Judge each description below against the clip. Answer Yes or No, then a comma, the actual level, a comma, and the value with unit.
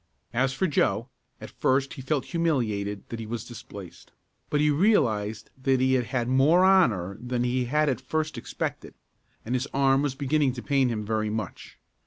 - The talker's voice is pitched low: Yes, low, 130 Hz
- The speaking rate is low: No, average, 185 wpm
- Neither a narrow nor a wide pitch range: Yes, average, 4.2 semitones